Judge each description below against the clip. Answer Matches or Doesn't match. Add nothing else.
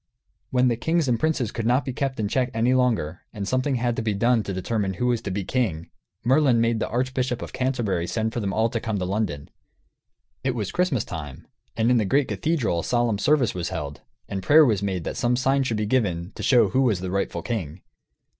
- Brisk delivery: Matches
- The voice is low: Matches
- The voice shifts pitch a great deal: Doesn't match